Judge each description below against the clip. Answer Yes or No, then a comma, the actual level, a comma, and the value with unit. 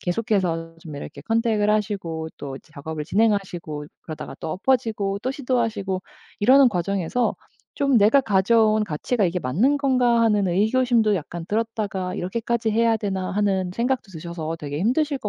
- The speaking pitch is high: Yes, high, 205 Hz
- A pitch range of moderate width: Yes, average, 4.8 semitones